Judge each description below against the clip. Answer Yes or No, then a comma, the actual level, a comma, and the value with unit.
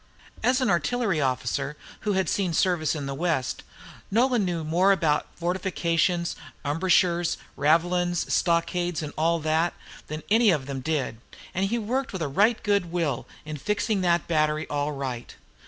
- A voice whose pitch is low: No, medium, 170 Hz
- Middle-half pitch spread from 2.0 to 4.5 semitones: Yes, average, 3.8 semitones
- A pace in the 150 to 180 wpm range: Yes, average, 165 wpm